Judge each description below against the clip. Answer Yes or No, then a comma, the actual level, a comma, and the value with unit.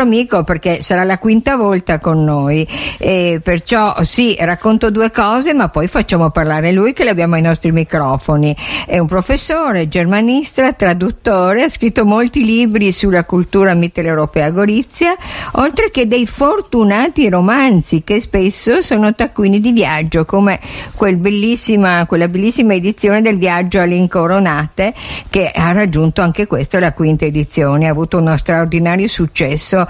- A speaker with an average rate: Yes, average, 145 wpm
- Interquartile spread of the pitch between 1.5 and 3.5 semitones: No, average, 4.8 semitones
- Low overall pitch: No, medium, 185 Hz